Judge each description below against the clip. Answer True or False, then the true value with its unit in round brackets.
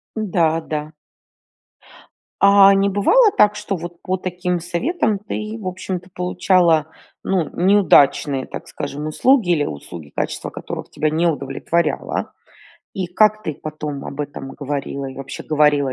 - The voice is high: False (175 Hz)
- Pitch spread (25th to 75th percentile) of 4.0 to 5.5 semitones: True (4.8 semitones)